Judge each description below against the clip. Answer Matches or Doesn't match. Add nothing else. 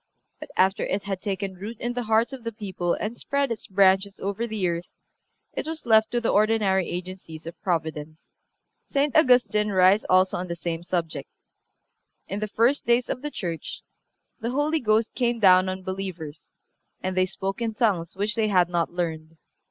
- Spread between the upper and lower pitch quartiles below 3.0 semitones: Doesn't match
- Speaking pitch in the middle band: Doesn't match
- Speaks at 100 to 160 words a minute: Doesn't match